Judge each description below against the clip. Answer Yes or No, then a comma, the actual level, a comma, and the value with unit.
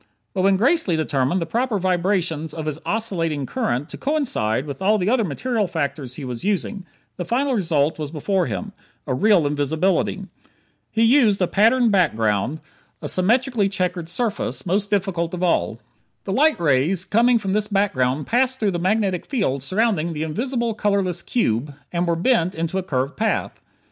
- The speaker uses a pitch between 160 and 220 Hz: Yes, medium, 185 Hz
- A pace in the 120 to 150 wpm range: No, average, 170 wpm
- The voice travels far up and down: Yes, wide, 5.7 semitones